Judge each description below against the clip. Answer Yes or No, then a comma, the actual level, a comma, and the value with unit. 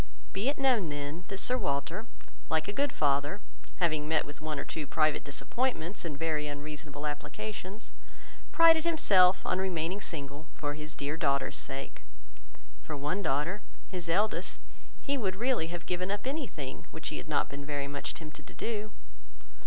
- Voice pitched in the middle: Yes, medium, 165 Hz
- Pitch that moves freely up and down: Yes, wide, 5.7 semitones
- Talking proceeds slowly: No, average, 170 wpm